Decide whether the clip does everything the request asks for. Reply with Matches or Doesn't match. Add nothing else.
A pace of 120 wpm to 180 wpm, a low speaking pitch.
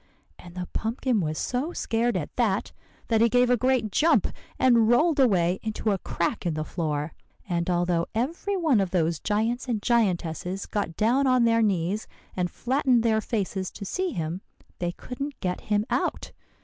Doesn't match